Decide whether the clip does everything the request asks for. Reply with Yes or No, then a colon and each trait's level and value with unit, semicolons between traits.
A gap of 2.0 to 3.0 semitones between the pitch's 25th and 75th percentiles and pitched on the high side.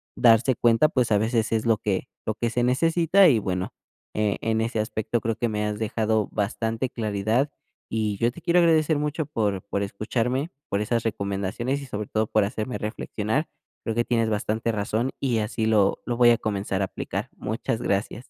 No: narrow, 2.6 semitones; low, 110 Hz